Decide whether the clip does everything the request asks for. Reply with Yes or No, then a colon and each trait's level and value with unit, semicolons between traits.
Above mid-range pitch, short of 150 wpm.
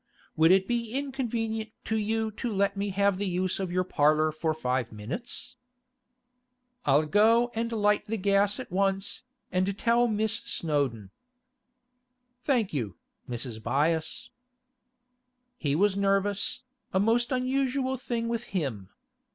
Yes: high, 200 Hz; slow, 135 wpm